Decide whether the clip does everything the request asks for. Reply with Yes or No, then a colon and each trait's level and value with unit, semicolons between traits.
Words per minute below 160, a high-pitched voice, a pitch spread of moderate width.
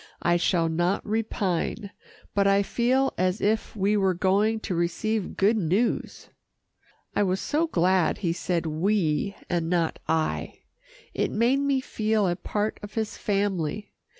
Yes: average, 150 wpm; high, 195 Hz; average, 3.8 semitones